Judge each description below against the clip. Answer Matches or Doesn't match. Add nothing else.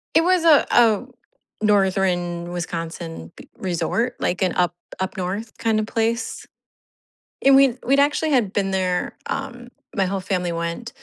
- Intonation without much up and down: Doesn't match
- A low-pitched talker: Doesn't match